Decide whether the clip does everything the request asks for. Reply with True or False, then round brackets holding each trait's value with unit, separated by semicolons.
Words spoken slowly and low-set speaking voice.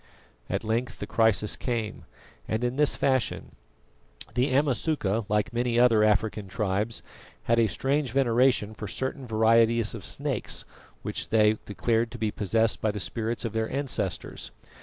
False (150 wpm; 115 Hz)